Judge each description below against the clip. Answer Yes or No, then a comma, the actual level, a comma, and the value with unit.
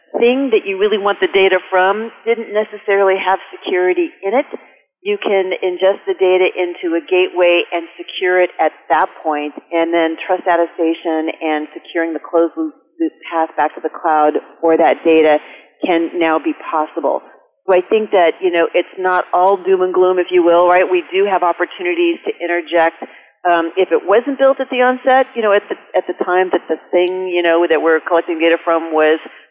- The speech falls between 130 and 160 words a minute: No, average, 195 wpm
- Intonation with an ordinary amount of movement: Yes, average, 3.1 semitones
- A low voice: No, medium, 180 Hz